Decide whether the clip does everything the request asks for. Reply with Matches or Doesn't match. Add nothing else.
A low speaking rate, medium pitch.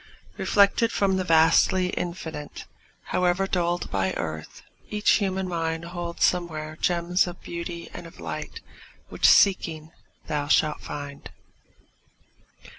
Matches